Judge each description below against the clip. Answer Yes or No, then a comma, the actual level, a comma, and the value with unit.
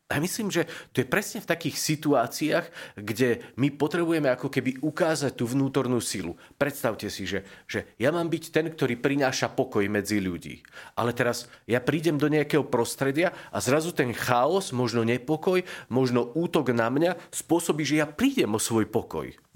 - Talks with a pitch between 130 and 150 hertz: Yes, medium, 140 Hz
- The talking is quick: Yes, fast, 170 wpm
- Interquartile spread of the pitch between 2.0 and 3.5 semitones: No, average, 4.8 semitones